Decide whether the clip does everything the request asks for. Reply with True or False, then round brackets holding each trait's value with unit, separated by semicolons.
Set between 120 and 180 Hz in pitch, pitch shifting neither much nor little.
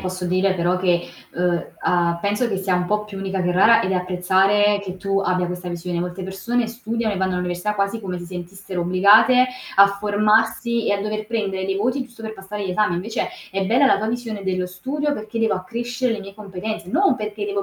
False (195 Hz; 3.1 semitones)